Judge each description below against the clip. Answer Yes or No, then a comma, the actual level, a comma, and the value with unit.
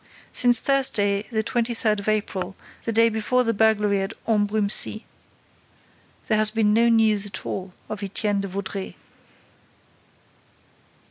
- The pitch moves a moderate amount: No, narrow, 2.0 semitones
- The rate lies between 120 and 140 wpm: Yes, slow, 135 wpm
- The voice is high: Yes, high, 215 Hz